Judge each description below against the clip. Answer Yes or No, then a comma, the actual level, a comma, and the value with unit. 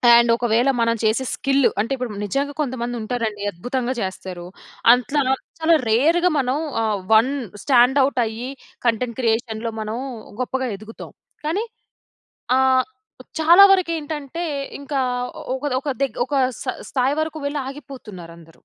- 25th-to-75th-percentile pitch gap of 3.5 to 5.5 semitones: Yes, average, 4.0 semitones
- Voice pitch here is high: Yes, very high, 255 Hz